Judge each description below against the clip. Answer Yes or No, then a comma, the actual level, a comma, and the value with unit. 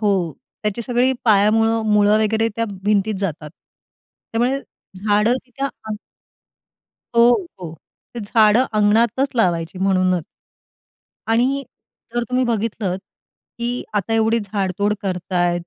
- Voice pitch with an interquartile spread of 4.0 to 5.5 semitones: No, average, 3.3 semitones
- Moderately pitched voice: No, high, 210 Hz